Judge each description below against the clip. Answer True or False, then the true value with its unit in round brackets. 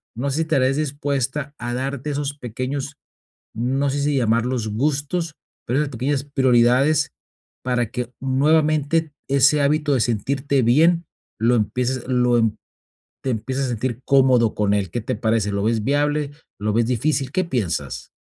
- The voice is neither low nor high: False (130 Hz)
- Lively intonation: False (3.4 semitones)